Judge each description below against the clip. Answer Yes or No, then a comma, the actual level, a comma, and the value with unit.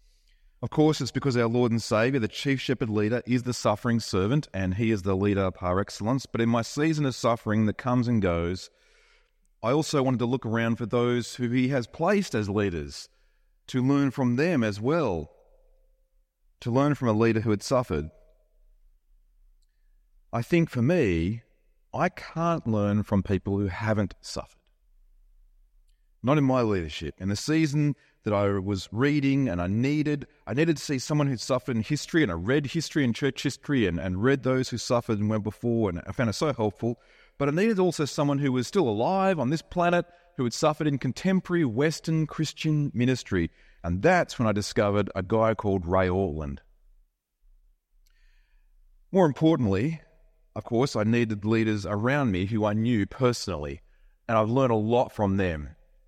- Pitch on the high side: No, low, 120 Hz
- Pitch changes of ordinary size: No, wide, 5.8 semitones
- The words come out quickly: No, average, 180 wpm